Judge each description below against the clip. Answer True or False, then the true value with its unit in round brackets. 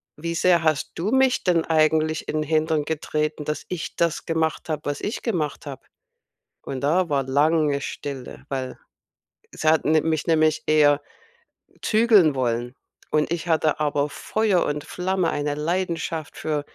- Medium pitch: True (155 Hz)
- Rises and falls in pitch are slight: True (2.3 semitones)